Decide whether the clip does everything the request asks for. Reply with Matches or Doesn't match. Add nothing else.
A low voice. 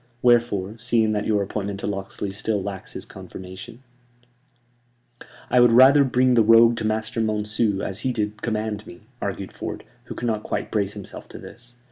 Matches